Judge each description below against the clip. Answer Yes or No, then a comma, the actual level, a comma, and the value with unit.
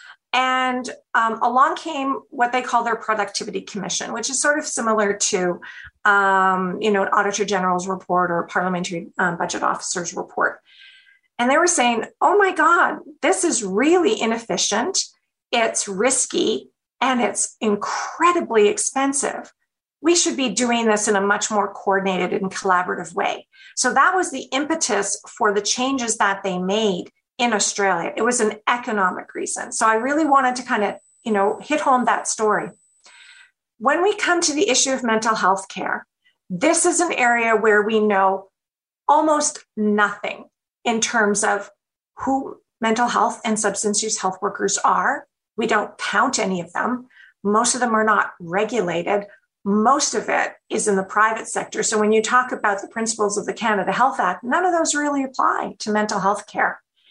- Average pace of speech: Yes, average, 170 wpm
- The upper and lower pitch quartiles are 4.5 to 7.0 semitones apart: Yes, average, 5.2 semitones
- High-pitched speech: Yes, high, 225 Hz